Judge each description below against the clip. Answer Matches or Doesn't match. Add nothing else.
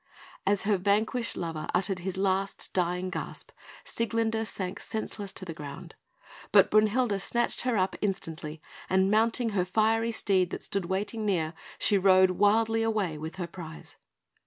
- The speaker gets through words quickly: Doesn't match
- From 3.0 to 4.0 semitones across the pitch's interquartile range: Matches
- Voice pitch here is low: Doesn't match